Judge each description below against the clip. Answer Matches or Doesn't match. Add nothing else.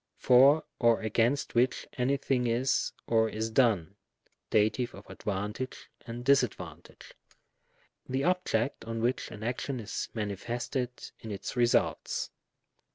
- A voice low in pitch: Matches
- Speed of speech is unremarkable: Doesn't match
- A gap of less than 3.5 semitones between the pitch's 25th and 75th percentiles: Matches